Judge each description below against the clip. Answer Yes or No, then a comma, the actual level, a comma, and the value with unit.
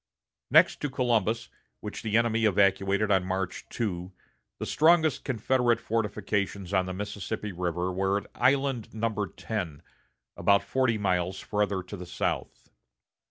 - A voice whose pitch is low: Yes, low, 105 Hz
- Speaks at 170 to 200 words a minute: No, slow, 135 wpm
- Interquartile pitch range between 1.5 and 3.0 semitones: No, average, 3.4 semitones